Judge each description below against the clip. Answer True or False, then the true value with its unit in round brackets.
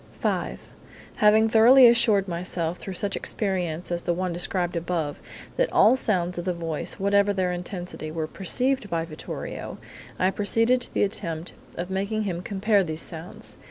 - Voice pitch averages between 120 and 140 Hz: False (185 Hz)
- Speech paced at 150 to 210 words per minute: True (160 wpm)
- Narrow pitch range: False (3.4 semitones)